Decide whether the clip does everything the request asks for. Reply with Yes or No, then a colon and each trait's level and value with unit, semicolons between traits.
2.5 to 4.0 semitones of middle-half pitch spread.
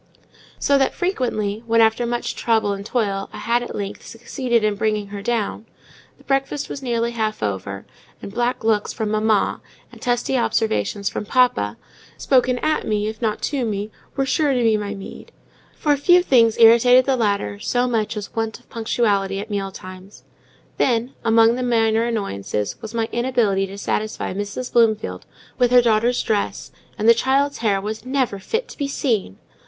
Yes: average, 3.1 semitones